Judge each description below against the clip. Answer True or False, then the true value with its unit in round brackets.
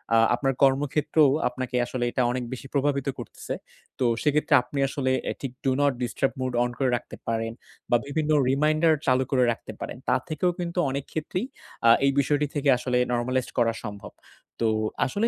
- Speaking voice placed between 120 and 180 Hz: True (135 Hz)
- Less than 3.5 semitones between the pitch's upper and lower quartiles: True (2.9 semitones)